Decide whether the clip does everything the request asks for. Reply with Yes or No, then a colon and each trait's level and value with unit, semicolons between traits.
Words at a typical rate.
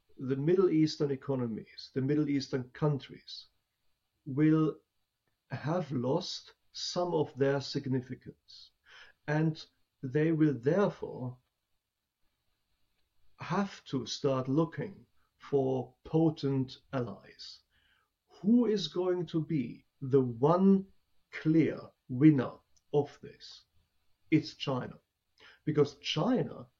No: slow, 90 wpm